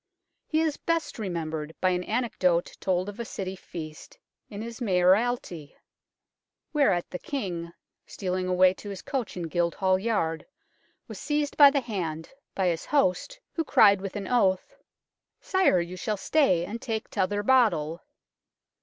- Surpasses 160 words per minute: No, average, 155 wpm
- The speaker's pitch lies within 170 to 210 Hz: Yes, high, 190 Hz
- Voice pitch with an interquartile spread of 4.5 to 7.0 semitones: Yes, average, 5.0 semitones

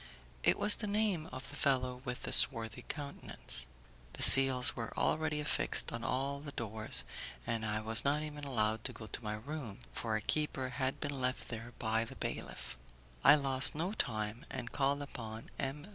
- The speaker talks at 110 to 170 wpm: No, average, 185 wpm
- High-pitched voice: No, low, 130 Hz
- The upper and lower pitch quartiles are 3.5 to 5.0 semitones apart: Yes, average, 4.3 semitones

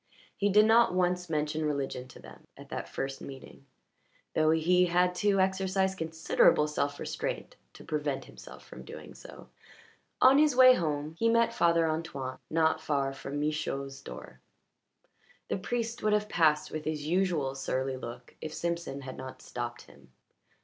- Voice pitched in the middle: Yes, medium, 155 Hz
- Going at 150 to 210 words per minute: Yes, average, 160 wpm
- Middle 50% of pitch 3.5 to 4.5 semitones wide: No, average, 5.3 semitones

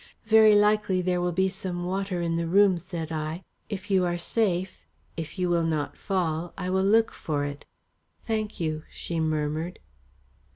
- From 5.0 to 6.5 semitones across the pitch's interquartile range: No, average, 2.9 semitones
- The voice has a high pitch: No, medium, 180 Hz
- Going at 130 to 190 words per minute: Yes, average, 170 wpm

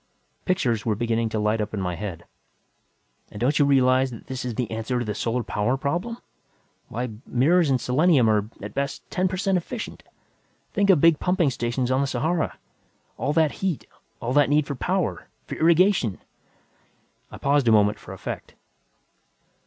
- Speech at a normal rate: Yes, average, 175 wpm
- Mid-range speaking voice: No, low, 130 Hz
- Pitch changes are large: Yes, wide, 6.0 semitones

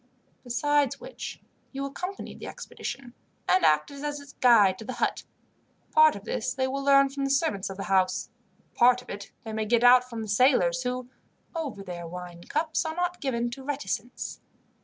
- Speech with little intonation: No, average, 5.1 semitones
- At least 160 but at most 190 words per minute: Yes, average, 185 wpm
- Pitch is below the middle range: No, very high, 250 Hz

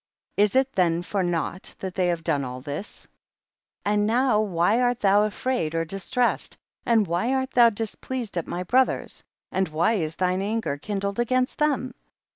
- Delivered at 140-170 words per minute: No, average, 180 wpm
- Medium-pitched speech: No, high, 200 Hz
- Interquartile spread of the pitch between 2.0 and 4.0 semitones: No, wide, 5.6 semitones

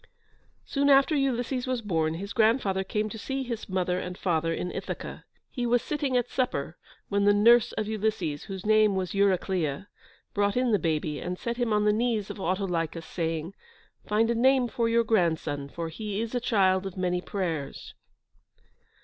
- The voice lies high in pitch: Yes, high, 205 Hz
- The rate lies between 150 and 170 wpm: No, average, 180 wpm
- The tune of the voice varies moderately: Yes, average, 4.6 semitones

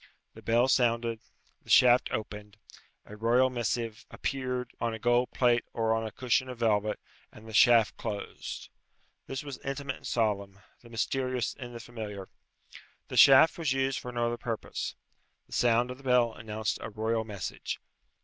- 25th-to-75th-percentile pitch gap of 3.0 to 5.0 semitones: No, narrow, 2.4 semitones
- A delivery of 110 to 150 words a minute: No, average, 170 wpm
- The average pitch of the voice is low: Yes, low, 120 Hz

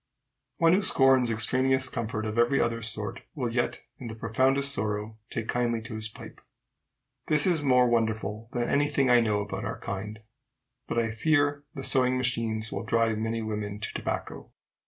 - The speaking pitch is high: No, low, 115 Hz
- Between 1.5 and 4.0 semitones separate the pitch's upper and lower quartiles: Yes, average, 3.2 semitones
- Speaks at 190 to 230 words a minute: No, average, 175 wpm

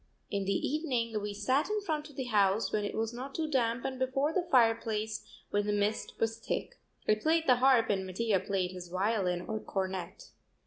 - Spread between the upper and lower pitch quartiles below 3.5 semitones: No, average, 4.5 semitones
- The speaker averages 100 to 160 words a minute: No, average, 200 wpm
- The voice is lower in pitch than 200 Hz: No, high, 225 Hz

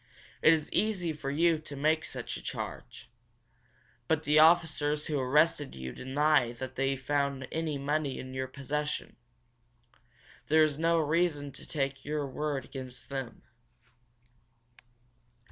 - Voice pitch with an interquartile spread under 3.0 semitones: Yes, narrow, 2.4 semitones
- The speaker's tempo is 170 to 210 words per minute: No, slow, 135 wpm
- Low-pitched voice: No, medium, 145 Hz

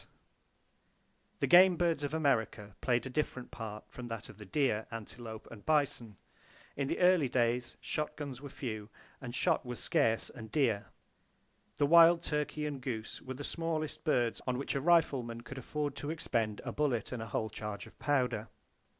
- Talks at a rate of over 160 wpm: Yes, average, 175 wpm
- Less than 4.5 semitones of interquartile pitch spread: No, average, 4.8 semitones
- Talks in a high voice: No, low, 130 Hz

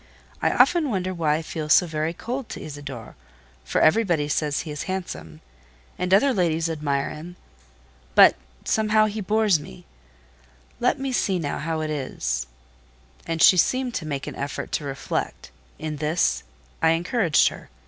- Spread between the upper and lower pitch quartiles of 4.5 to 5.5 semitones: Yes, average, 4.8 semitones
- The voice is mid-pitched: Yes, medium, 165 Hz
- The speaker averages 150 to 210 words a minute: Yes, average, 160 wpm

